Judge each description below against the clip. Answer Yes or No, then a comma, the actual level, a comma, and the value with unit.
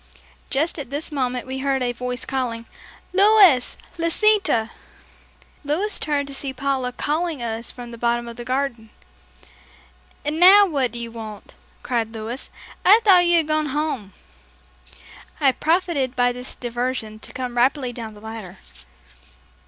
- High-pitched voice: Yes, very high, 260 Hz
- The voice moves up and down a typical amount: Yes, average, 4.3 semitones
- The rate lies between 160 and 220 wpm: No, average, 150 wpm